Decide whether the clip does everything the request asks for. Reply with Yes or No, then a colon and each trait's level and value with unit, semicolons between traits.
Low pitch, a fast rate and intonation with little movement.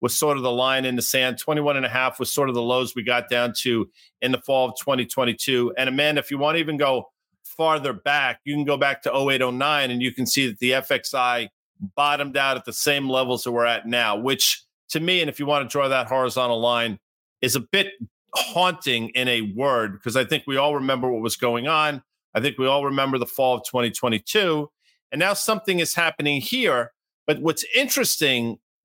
No: low, 130 Hz; fast, 220 wpm; average, 3.0 semitones